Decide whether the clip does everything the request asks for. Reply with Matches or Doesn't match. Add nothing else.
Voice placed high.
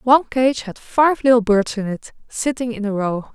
Matches